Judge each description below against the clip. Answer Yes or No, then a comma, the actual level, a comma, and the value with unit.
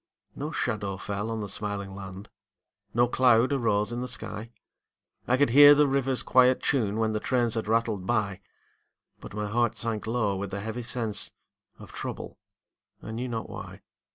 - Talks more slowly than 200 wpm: Yes, average, 175 wpm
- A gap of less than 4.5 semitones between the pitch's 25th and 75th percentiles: Yes, average, 3.2 semitones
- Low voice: Yes, low, 115 Hz